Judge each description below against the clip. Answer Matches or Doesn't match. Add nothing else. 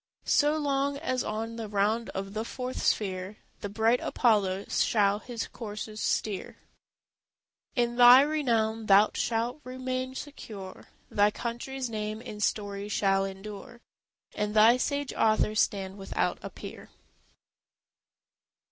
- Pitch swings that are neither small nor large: Matches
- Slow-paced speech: Matches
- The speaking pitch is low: Doesn't match